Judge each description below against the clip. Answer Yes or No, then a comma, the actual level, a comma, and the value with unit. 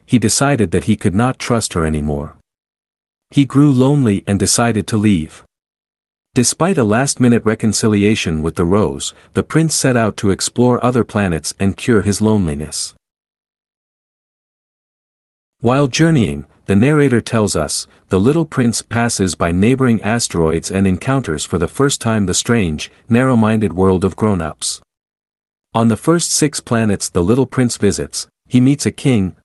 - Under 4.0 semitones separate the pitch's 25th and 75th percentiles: No, average, 4.6 semitones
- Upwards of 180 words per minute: No, average, 155 wpm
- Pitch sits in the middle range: No, low, 110 Hz